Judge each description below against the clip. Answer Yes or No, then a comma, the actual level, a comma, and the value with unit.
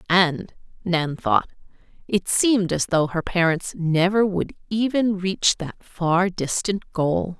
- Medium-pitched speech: Yes, medium, 180 Hz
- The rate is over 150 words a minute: No, average, 140 wpm